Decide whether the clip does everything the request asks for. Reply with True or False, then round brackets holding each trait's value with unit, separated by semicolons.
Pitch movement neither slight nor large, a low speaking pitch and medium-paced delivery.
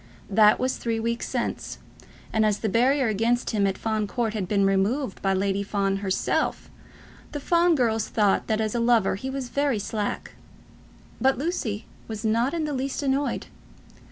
False (4.2 semitones; 225 Hz; 175 wpm)